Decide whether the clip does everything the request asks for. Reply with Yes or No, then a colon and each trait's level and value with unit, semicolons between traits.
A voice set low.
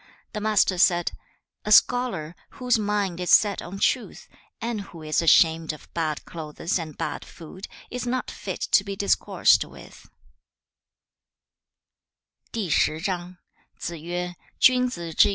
No: high, 190 Hz